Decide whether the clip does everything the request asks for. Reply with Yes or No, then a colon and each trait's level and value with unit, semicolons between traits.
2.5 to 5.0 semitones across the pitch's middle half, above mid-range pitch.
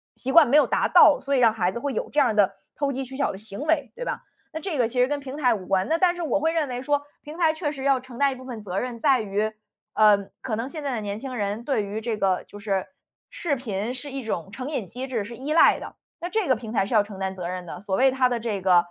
No: wide, 5.4 semitones; high, 245 Hz